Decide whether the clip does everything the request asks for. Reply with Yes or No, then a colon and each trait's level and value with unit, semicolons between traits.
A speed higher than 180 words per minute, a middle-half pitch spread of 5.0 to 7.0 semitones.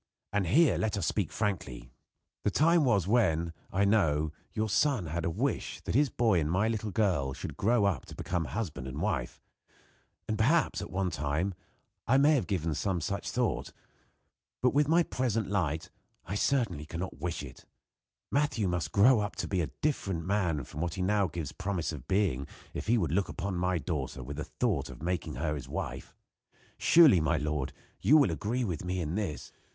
Yes: average, 190 wpm; wide, 5.6 semitones